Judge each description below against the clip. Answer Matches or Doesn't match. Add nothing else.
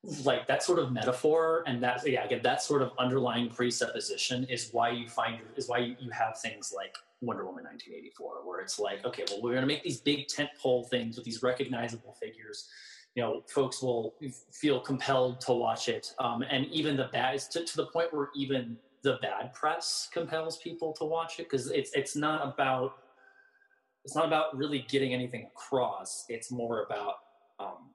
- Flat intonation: Doesn't match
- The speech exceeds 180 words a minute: Matches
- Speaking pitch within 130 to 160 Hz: Matches